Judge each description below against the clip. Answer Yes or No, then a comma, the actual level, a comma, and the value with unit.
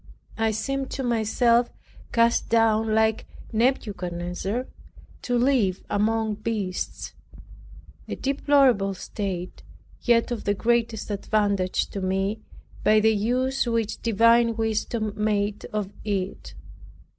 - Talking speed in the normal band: No, slow, 110 wpm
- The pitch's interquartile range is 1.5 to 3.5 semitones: Yes, narrow, 2.5 semitones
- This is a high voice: Yes, high, 220 Hz